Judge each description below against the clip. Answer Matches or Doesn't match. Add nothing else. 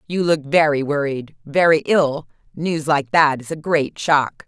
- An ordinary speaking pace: Matches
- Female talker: Matches